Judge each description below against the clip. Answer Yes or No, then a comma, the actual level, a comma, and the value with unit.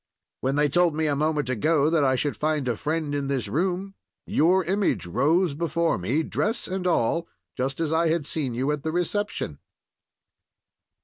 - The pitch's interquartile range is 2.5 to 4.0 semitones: Yes, average, 3.4 semitones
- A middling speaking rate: Yes, average, 180 wpm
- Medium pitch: Yes, medium, 155 Hz